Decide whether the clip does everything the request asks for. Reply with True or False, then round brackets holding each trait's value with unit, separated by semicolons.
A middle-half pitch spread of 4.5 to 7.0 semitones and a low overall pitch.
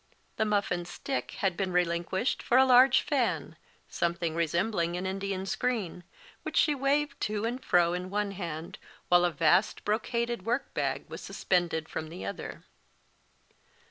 False (5.4 semitones; 190 Hz)